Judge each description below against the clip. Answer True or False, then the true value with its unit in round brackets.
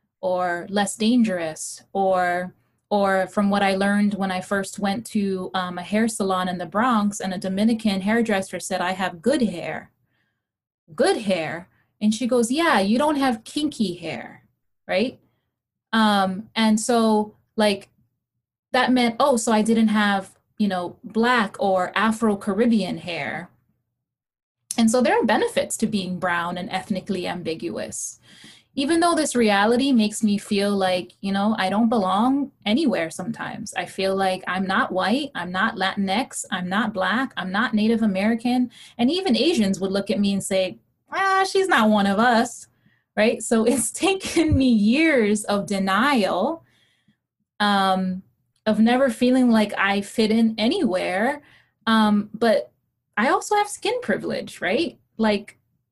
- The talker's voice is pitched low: False (210 Hz)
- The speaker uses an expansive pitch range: False (3.9 semitones)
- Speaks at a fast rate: False (155 wpm)